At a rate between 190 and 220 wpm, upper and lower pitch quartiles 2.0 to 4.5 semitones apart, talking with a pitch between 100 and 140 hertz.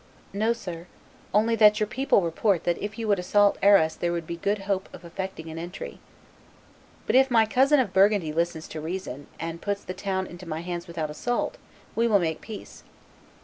No: average, 195 wpm; average, 3.9 semitones; high, 190 Hz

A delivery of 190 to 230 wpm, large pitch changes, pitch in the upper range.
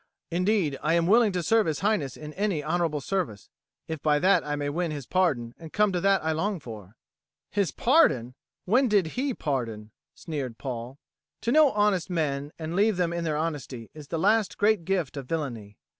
No: average, 195 wpm; wide, 5.7 semitones; medium, 165 Hz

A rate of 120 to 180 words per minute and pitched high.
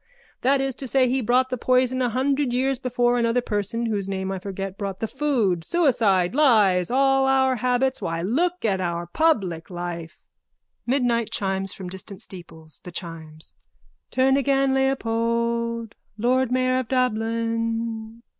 Yes: average, 150 wpm; high, 235 Hz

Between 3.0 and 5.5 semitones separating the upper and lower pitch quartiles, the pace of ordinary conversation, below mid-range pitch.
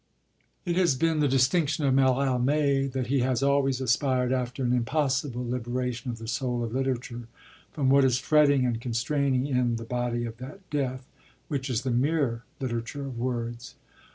No: narrow, 2.4 semitones; average, 170 wpm; low, 130 Hz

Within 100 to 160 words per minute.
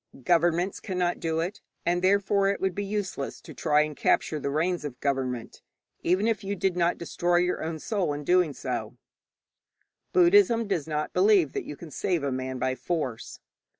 No: average, 185 wpm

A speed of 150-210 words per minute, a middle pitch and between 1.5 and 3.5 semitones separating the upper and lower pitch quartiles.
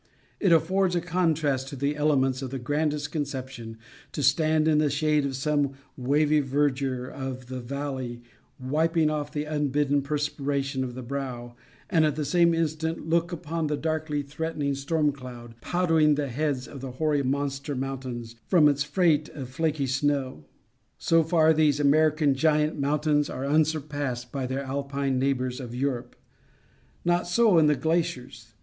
Yes: average, 160 wpm; medium, 145 Hz; average, 2.7 semitones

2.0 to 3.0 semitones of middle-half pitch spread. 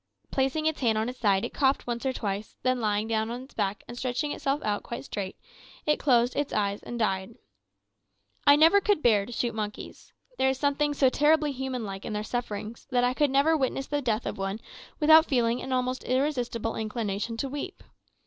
No: average, 4.3 semitones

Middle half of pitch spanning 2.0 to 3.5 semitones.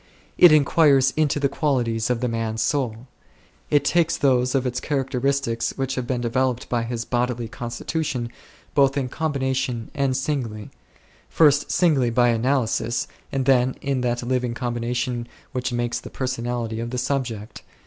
Yes: narrow, 2.4 semitones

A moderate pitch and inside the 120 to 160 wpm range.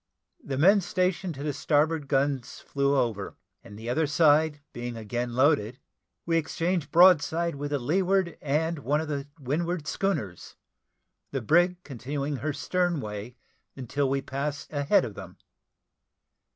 Yes: medium, 145 Hz; average, 150 wpm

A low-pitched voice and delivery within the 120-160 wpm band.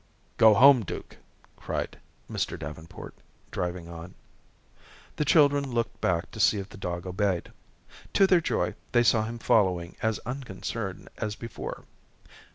Yes: low, 105 Hz; average, 140 wpm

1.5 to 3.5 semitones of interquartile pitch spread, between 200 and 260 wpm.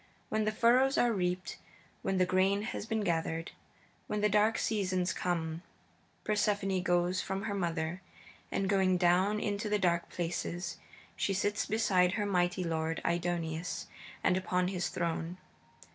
No: average, 2.8 semitones; average, 145 wpm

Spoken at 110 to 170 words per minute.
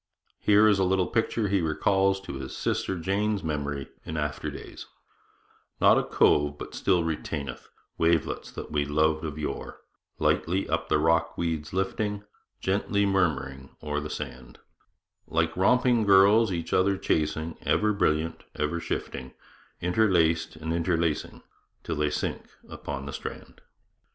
Yes: average, 140 wpm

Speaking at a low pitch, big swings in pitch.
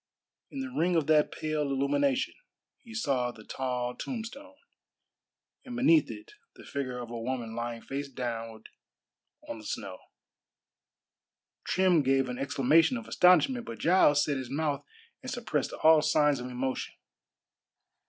No: medium, 145 Hz; wide, 7.1 semitones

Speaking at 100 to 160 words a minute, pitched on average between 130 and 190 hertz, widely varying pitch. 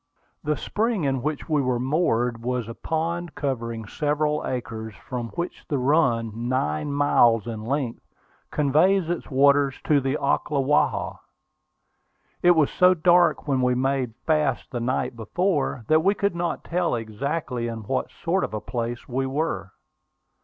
No: average, 155 wpm; low, 135 Hz; average, 4.7 semitones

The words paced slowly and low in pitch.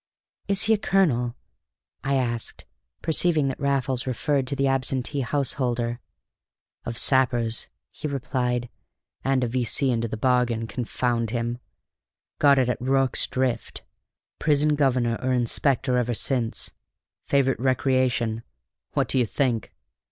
Yes: slow, 130 wpm; low, 130 Hz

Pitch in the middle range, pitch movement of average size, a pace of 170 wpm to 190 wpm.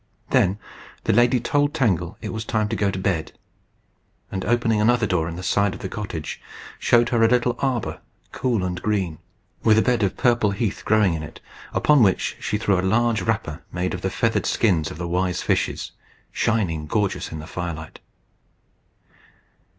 No: low, 105 Hz; average, 4.2 semitones; average, 180 wpm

